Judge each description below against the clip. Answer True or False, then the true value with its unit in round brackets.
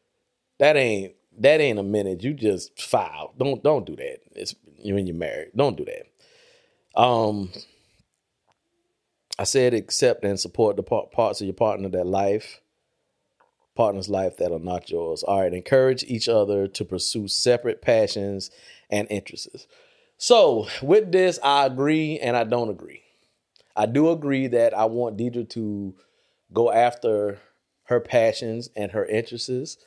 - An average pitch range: False (7.3 semitones)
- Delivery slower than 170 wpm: True (150 wpm)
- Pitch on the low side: True (120 Hz)